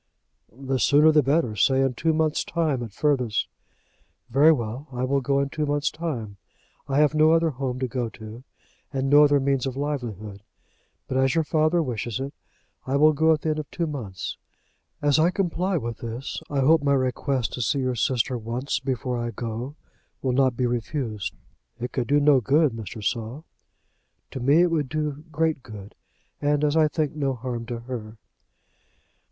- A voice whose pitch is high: No, low, 135 Hz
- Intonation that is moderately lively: Yes, average, 3.7 semitones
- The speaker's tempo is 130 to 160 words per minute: No, average, 190 wpm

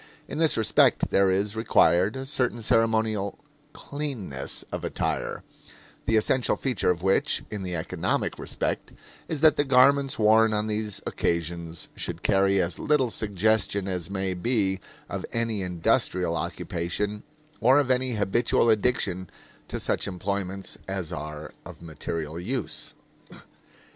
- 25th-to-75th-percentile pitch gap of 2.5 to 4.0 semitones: No, average, 4.4 semitones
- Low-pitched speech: Yes, low, 100 Hz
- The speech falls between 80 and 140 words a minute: Yes, slow, 135 wpm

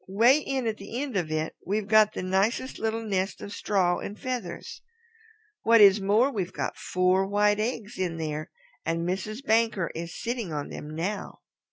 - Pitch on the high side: Yes, high, 205 Hz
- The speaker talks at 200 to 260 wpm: No, average, 180 wpm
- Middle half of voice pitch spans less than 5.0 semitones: Yes, average, 3.6 semitones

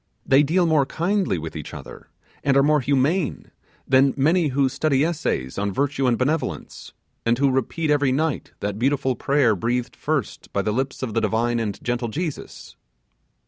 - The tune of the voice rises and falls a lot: No, average, 3.9 semitones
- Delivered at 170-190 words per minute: Yes, average, 175 wpm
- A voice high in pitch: No, low, 135 Hz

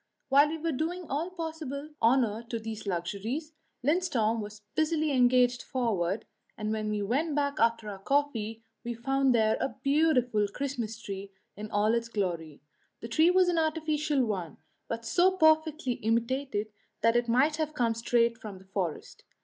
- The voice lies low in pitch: No, high, 240 Hz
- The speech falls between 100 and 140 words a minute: No, average, 165 wpm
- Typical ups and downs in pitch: No, wide, 5.8 semitones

